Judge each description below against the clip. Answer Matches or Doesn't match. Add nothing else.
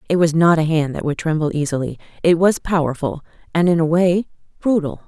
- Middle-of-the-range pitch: Matches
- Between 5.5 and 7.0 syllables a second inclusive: Matches